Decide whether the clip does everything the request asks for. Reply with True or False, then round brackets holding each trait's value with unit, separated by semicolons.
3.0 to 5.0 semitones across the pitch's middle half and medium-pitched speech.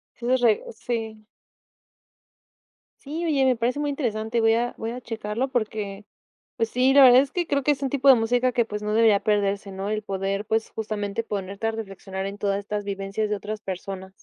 False (3.4 semitones; 220 Hz)